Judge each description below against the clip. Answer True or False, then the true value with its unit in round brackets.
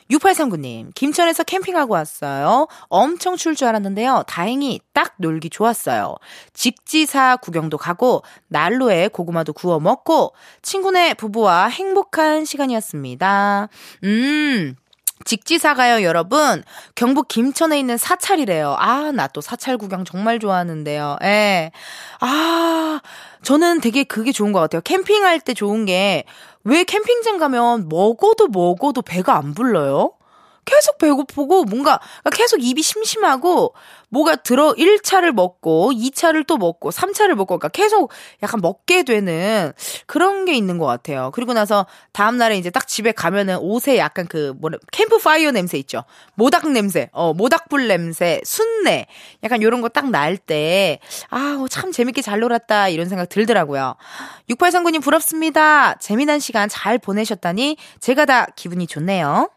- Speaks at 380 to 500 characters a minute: False (300 characters per minute)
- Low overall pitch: False (245 Hz)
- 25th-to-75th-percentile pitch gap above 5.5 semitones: True (8.3 semitones)